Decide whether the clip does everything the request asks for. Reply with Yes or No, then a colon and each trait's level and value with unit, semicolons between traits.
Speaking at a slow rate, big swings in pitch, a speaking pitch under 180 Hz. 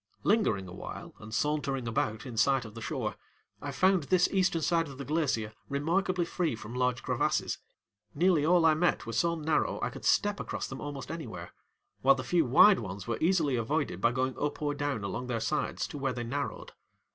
No: fast, 205 wpm; wide, 5.8 semitones; medium, 140 Hz